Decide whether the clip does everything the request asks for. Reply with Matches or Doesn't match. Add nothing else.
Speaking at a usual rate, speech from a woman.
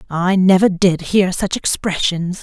Matches